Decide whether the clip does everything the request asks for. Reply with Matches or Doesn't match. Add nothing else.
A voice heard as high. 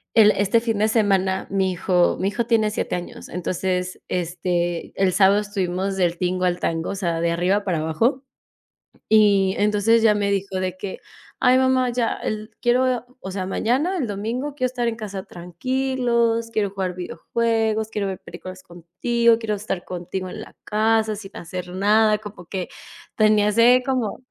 Matches